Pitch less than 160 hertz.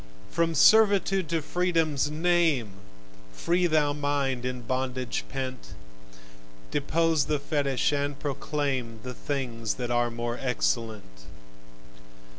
Yes: medium, 140 Hz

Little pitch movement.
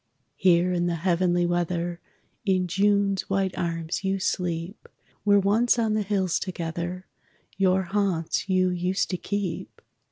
Yes: narrow, 2.1 semitones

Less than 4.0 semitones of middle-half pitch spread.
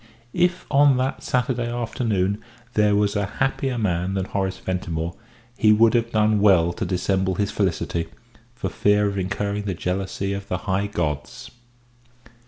Yes: average, 3.5 semitones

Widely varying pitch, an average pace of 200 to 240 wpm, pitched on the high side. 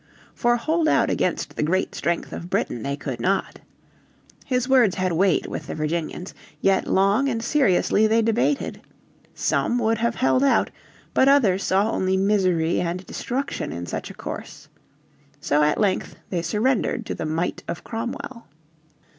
No: wide, 5.7 semitones; average, 160 wpm; high, 195 Hz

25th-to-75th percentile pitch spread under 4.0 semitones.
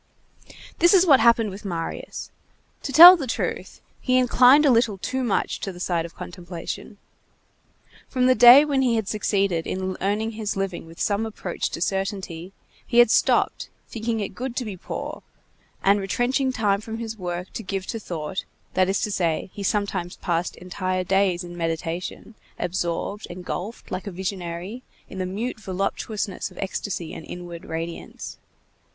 No: average, 4.3 semitones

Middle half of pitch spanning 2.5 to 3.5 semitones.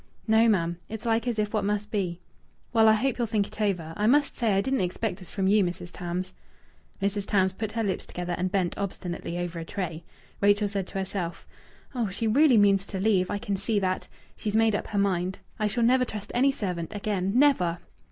Yes: average, 3.1 semitones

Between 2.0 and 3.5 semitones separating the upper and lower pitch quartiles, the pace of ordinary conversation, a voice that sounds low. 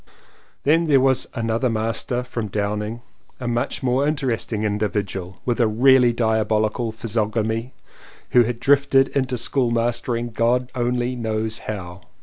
Yes: narrow, 2.5 semitones; average, 150 wpm; low, 115 Hz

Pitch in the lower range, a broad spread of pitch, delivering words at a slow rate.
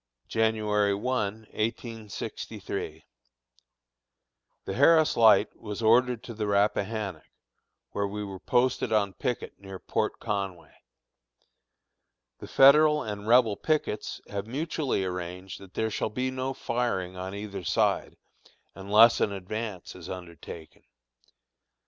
No: low, 105 Hz; average, 3.5 semitones; slow, 115 wpm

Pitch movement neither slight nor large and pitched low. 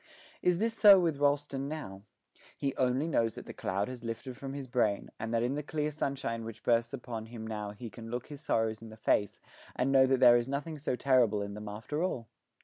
Yes: average, 4.0 semitones; low, 125 Hz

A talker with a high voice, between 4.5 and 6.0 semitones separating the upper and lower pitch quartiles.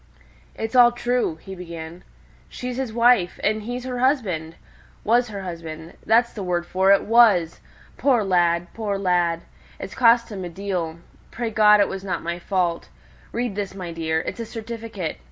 Yes: high, 200 Hz; average, 5.1 semitones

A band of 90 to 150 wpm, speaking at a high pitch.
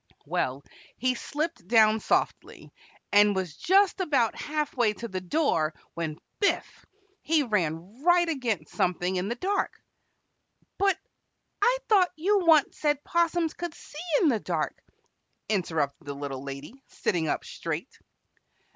Yes: average, 140 wpm; high, 235 Hz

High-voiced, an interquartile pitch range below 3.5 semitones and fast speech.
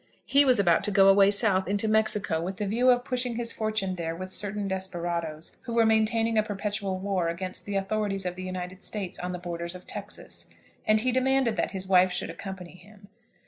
Yes: high, 195 Hz; average, 3.0 semitones; fast, 210 wpm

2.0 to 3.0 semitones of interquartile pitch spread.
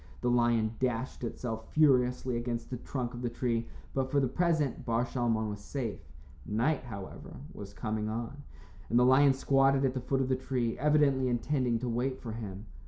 Yes: narrow, 2.5 semitones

